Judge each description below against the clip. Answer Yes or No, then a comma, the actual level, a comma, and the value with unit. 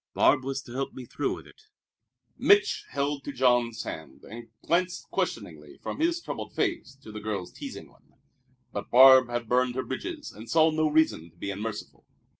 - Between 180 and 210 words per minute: Yes, average, 185 wpm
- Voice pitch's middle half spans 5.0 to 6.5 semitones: Yes, wide, 5.5 semitones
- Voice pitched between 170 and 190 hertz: No, low, 130 Hz